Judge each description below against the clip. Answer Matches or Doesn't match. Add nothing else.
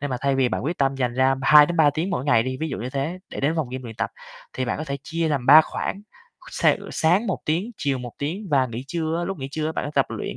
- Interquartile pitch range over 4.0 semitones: Doesn't match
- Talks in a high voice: Doesn't match